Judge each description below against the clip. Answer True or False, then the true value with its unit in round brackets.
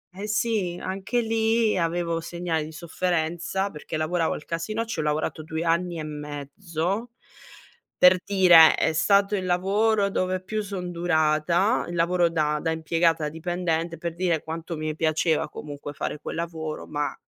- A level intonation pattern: False (3.0 semitones)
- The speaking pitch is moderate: True (170 Hz)